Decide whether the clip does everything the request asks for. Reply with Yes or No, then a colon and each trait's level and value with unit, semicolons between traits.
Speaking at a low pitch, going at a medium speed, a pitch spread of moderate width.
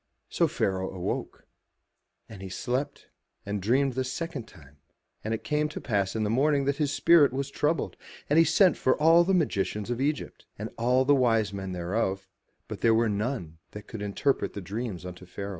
No: low, 115 Hz; average, 190 wpm; wide, 6.1 semitones